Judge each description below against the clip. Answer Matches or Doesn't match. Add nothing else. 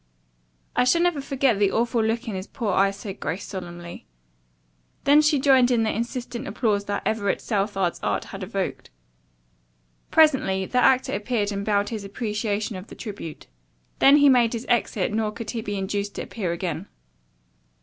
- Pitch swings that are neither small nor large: Matches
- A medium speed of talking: Matches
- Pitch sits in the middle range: Doesn't match